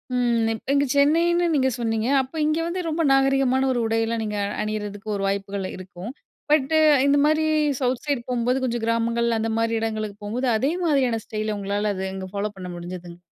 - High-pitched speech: Yes, high, 230 Hz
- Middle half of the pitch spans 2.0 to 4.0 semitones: No, average, 4.4 semitones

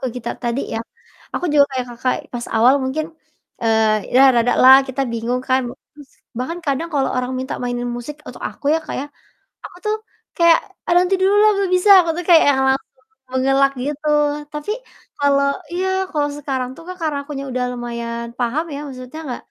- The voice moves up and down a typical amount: Yes, average, 3.9 semitones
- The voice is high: Yes, very high, 270 Hz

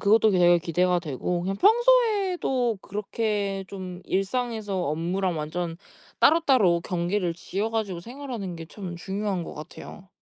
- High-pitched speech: Yes, high, 195 Hz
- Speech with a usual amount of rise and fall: Yes, average, 4.2 semitones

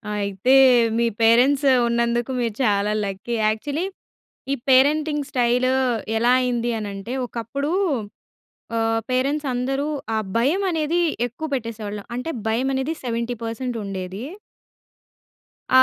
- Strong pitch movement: No, average, 3.2 semitones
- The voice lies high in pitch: Yes, high, 240 Hz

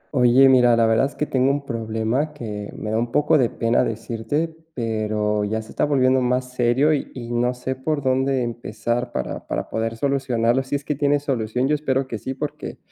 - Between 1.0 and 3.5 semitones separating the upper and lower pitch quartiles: Yes, average, 3.2 semitones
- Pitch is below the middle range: Yes, low, 125 Hz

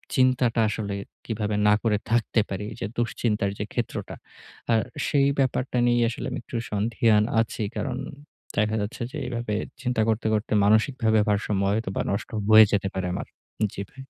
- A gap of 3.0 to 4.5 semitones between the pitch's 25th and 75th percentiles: No, narrow, 2.4 semitones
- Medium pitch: No, low, 110 Hz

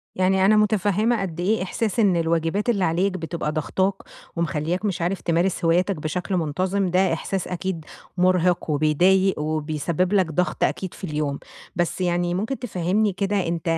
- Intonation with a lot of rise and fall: No, average, 2.7 semitones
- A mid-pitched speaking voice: Yes, medium, 180 Hz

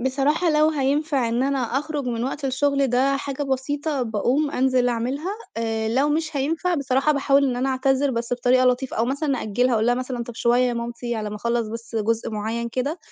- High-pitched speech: Yes, very high, 260 Hz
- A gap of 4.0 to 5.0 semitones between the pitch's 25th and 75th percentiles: No, average, 3.0 semitones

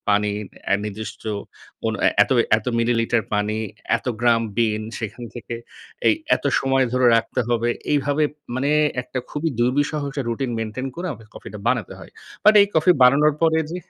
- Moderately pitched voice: No, low, 125 Hz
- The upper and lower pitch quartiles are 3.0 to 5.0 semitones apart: Yes, average, 4.2 semitones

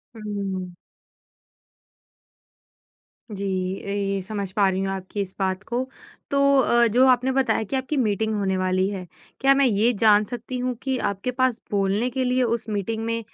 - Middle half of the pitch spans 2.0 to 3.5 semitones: No, average, 4.4 semitones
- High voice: Yes, high, 215 Hz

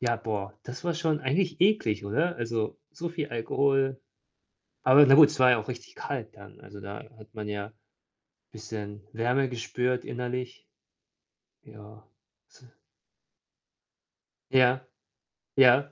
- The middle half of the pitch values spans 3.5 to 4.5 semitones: Yes, average, 4.1 semitones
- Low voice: Yes, low, 125 Hz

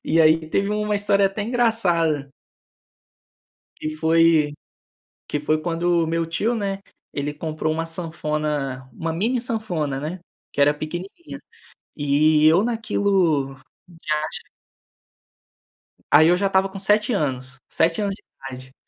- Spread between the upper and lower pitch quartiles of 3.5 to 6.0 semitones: Yes, average, 4.5 semitones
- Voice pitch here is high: No, medium, 165 Hz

